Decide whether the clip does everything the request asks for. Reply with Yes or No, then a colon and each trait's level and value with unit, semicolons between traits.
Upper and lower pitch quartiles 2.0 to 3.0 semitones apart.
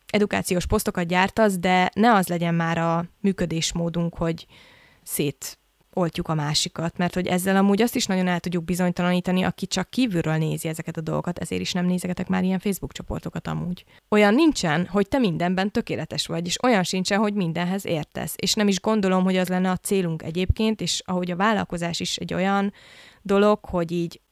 Yes: narrow, 2.5 semitones